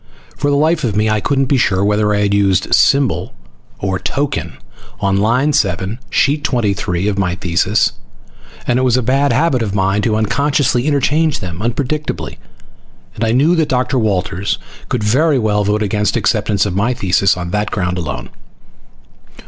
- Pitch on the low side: Yes, low, 110 Hz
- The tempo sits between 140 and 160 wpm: No, average, 175 wpm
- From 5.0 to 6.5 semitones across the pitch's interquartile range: Yes, wide, 5.5 semitones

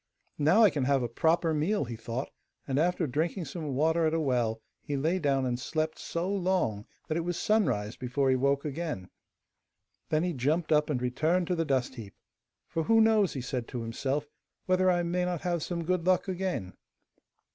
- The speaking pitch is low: No, medium, 155 Hz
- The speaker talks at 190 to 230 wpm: Yes, average, 200 wpm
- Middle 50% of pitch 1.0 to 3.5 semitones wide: No, average, 5.1 semitones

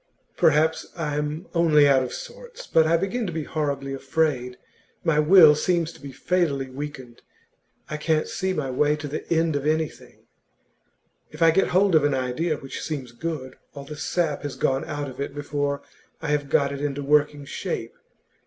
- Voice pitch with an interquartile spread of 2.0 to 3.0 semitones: Yes, narrow, 2.6 semitones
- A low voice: No, medium, 150 Hz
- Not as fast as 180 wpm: No, average, 185 wpm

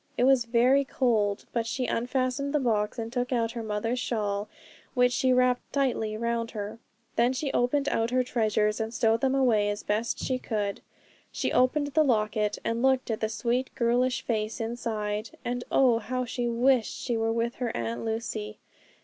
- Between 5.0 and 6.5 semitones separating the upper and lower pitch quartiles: No, narrow, 2.5 semitones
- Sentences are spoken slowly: No, average, 185 wpm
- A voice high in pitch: Yes, high, 235 Hz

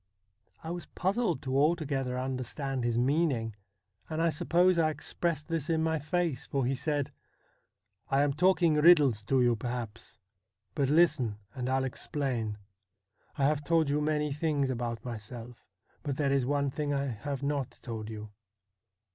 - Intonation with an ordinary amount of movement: Yes, average, 3.9 semitones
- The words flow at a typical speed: Yes, average, 160 wpm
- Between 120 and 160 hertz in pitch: Yes, medium, 140 Hz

